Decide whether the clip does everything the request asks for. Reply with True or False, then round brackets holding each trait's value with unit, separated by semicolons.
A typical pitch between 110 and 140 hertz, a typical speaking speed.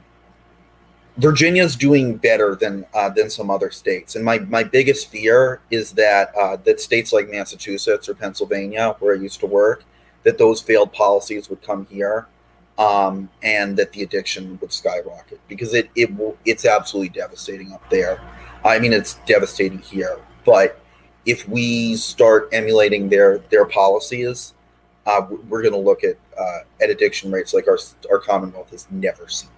True (135 Hz; 165 wpm)